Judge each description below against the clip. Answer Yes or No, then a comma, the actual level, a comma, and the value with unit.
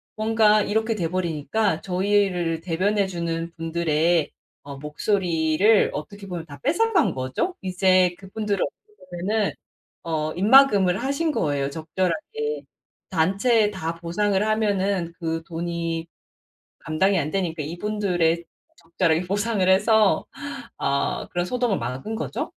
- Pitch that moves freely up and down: No, average, 4.3 semitones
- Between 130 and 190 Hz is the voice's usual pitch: Yes, medium, 185 Hz